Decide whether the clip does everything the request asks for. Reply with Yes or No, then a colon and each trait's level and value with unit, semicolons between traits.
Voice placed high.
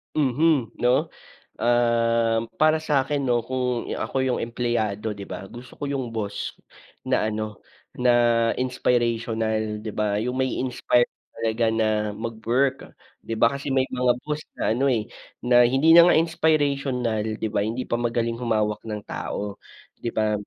No: low, 120 Hz